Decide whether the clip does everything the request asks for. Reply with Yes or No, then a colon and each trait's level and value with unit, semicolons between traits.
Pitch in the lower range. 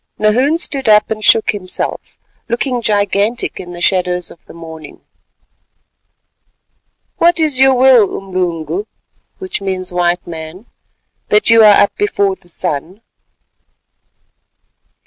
No: high, 205 Hz